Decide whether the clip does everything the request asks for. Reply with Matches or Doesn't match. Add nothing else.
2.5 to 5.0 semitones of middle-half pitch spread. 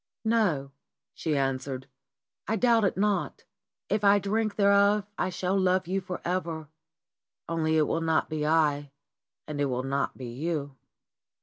Doesn't match